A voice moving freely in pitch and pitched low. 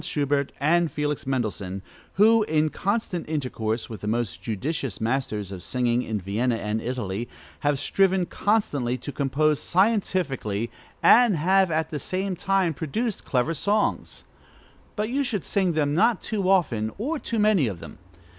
No: wide, 8.5 semitones; medium, 150 Hz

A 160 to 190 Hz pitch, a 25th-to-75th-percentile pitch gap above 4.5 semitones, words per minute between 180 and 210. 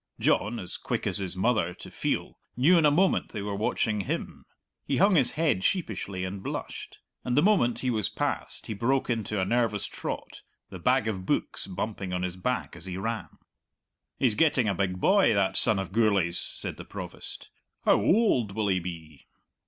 No: low, 105 Hz; average, 4.9 semitones; average, 190 wpm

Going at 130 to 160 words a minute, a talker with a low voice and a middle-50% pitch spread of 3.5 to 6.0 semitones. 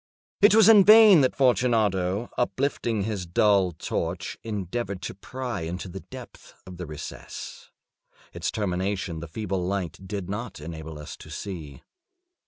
Yes: average, 145 wpm; low, 100 Hz; average, 5.3 semitones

